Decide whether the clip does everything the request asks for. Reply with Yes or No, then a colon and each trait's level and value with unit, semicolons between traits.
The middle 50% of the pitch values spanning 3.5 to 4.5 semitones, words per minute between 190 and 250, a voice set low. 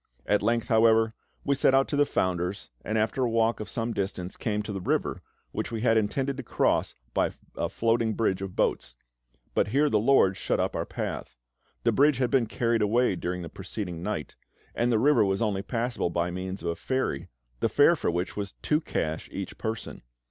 Yes: average, 3.9 semitones; fast, 205 wpm; low, 110 Hz